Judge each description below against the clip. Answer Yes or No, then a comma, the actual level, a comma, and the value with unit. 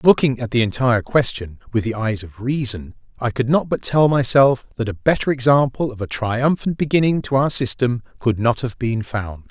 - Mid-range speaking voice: No, low, 125 Hz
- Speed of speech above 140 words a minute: Yes, average, 200 wpm